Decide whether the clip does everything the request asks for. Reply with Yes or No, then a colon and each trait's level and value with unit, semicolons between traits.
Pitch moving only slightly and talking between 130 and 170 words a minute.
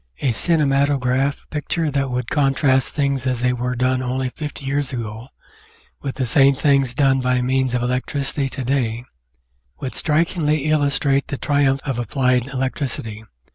Yes: narrow, 2.0 semitones; average, 150 wpm